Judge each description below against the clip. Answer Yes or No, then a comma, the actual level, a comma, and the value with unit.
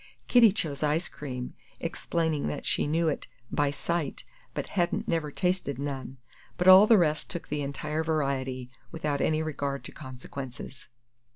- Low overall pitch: No, medium, 150 Hz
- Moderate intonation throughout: Yes, average, 3.2 semitones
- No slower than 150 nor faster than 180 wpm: Yes, average, 155 wpm